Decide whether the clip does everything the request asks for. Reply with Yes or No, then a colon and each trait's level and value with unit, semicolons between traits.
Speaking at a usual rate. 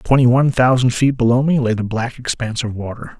No: fast, 225 wpm